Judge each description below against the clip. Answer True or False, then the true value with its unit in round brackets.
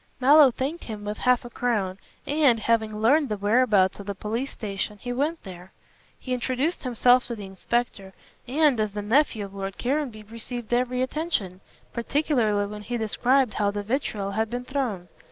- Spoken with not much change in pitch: False (3.8 semitones)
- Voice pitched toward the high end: True (230 Hz)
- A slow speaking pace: False (175 wpm)